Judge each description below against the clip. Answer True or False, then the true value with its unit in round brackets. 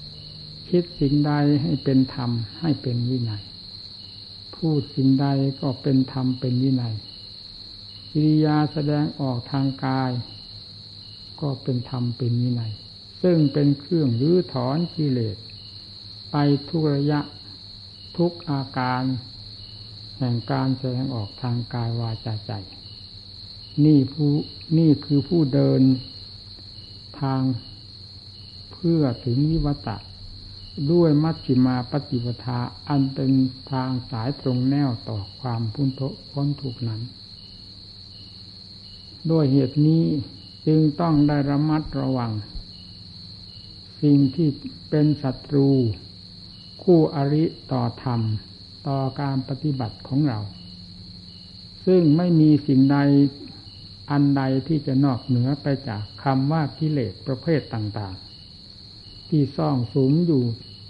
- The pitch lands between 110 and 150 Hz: True (125 Hz)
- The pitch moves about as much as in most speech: False (5.9 semitones)